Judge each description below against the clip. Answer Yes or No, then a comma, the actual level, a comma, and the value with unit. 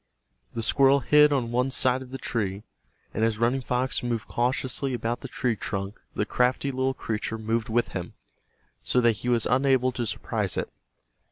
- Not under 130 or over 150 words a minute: No, average, 180 wpm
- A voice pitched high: No, low, 125 Hz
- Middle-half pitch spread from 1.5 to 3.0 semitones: Yes, narrow, 2.6 semitones